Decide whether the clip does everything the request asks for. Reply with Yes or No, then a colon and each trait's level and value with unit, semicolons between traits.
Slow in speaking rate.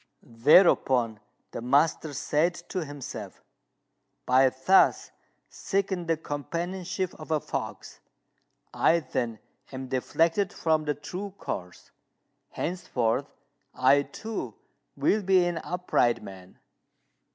Yes: slow, 105 wpm